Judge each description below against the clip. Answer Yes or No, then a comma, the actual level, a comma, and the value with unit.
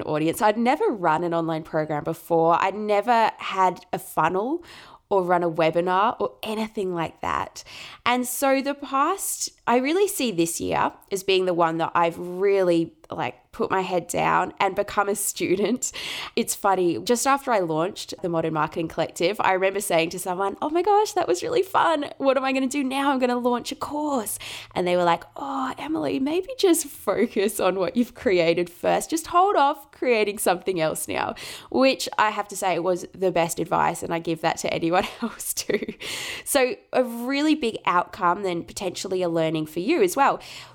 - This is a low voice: No, high, 200 Hz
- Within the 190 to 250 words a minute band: Yes, average, 195 wpm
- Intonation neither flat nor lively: No, wide, 8.0 semitones